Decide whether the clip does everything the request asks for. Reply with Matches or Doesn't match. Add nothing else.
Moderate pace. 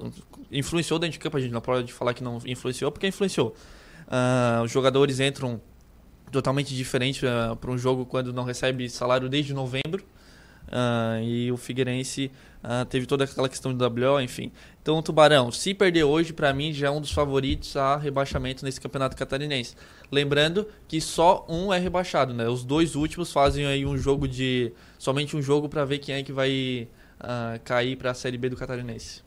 Doesn't match